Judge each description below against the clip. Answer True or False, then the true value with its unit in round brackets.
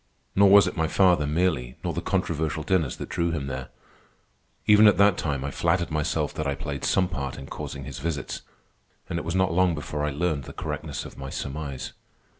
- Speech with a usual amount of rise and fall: True (4.3 semitones)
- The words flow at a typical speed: False (210 wpm)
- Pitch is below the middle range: True (80 Hz)